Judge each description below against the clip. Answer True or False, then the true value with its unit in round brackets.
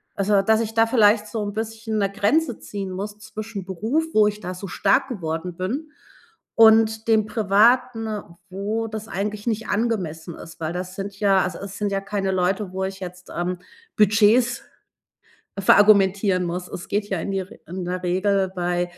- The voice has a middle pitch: False (200 Hz)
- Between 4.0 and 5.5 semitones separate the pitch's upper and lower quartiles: False (2.9 semitones)